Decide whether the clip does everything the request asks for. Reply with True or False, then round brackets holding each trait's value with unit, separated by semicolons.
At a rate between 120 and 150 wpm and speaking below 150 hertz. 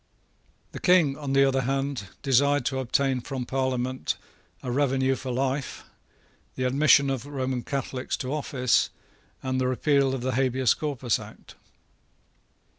True (145 wpm; 135 Hz)